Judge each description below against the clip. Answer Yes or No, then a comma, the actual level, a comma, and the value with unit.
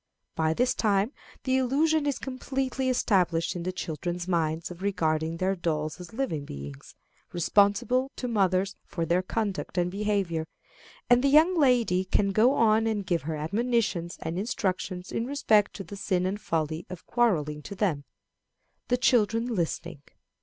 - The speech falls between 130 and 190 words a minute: Yes, average, 160 wpm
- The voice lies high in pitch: Yes, high, 195 Hz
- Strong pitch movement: Yes, wide, 5.8 semitones